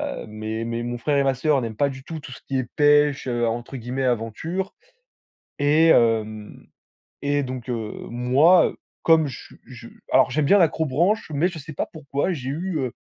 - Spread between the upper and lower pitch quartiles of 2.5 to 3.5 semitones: No, average, 4.3 semitones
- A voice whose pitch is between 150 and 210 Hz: No, low, 135 Hz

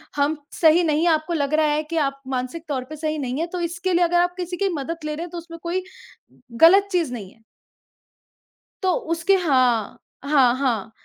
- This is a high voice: Yes, very high, 310 Hz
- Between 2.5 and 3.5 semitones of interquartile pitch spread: No, average, 4.1 semitones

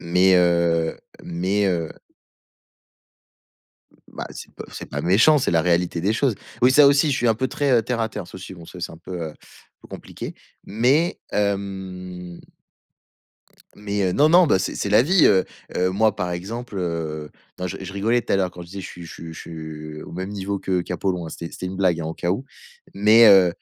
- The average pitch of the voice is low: Yes, very low, 95 Hz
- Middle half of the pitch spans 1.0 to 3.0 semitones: No, average, 3.7 semitones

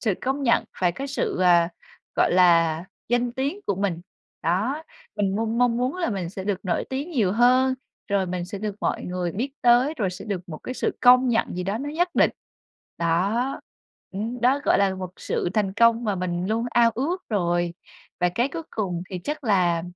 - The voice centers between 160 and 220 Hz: Yes, high, 210 Hz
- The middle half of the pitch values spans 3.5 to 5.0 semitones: No, wide, 5.5 semitones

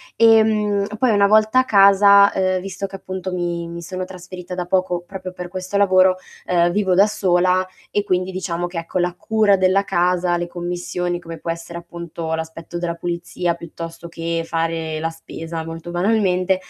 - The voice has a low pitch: No, medium, 180 Hz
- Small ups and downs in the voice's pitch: Yes, narrow, 2.2 semitones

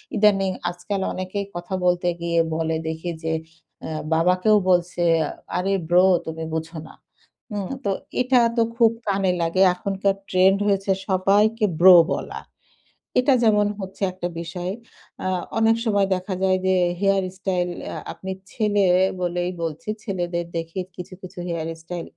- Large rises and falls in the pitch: No, narrow, 2.4 semitones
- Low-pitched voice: No, medium, 185 Hz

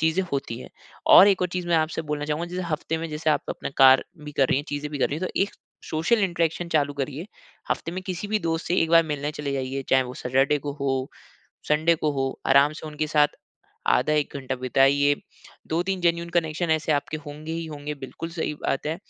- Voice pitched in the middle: Yes, medium, 155 Hz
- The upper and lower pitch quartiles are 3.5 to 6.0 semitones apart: No, average, 2.8 semitones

